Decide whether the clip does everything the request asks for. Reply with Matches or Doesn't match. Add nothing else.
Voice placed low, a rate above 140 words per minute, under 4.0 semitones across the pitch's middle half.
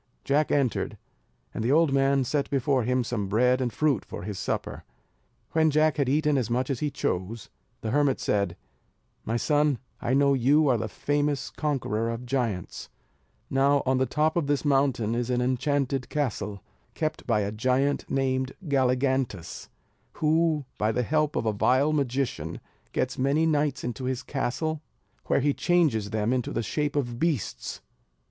Matches